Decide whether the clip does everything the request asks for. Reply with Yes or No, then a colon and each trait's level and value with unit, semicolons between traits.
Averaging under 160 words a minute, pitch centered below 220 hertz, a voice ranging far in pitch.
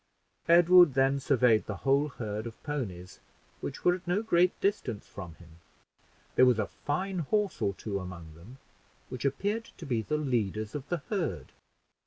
No: average, 170 wpm; low, 135 Hz; wide, 8.4 semitones